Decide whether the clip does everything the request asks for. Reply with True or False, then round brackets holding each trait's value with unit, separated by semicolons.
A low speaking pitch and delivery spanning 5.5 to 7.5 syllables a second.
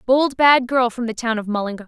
False (240 Hz; 5.6 syllables/s)